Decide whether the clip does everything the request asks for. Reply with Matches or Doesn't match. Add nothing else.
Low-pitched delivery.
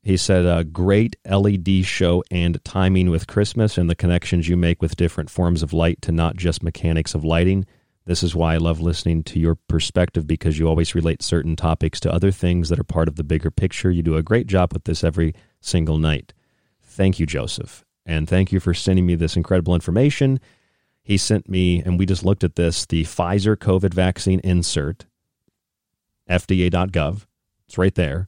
Matches